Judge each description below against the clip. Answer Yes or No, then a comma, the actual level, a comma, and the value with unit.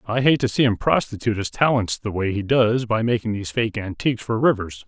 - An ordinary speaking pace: No, fast, 235 wpm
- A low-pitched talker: Yes, low, 110 Hz